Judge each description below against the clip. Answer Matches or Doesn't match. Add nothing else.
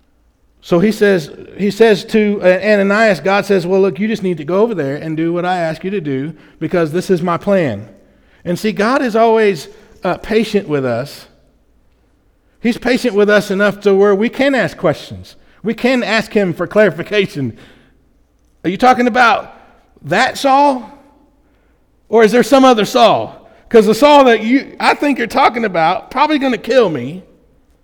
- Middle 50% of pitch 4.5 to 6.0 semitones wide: Matches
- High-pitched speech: Matches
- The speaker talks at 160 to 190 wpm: Matches